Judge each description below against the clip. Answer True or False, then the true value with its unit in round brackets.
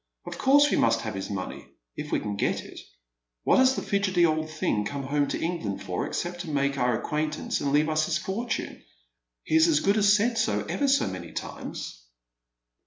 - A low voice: False (155 Hz)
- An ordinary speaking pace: False (215 wpm)